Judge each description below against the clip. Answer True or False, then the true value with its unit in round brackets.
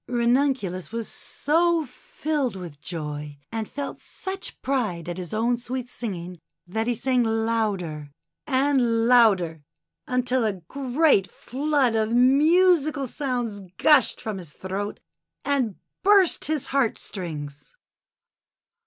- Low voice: False (235 Hz)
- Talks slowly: True (120 wpm)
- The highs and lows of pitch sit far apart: True (6.5 semitones)